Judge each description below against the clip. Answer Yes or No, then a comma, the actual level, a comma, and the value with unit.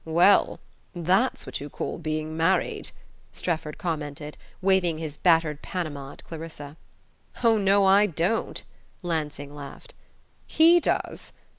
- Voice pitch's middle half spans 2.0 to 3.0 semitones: No, average, 4.0 semitones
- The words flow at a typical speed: No, slow, 120 wpm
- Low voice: No, medium, 165 Hz